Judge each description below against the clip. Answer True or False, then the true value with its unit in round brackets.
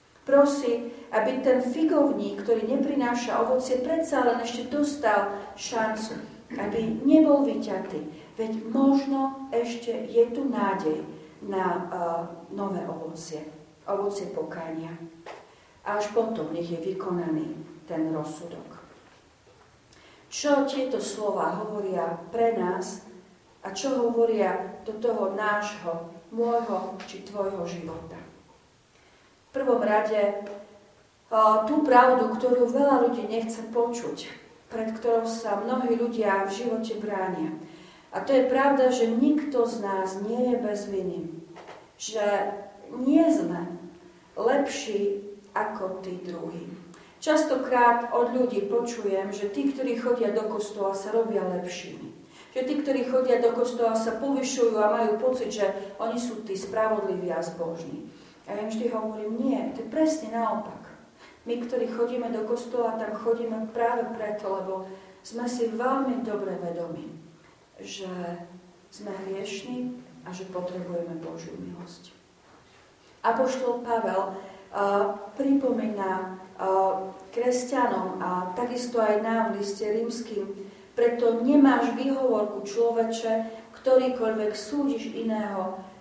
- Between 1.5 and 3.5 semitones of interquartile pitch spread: False (4.1 semitones)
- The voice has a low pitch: False (220 Hz)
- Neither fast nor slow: True (120 wpm)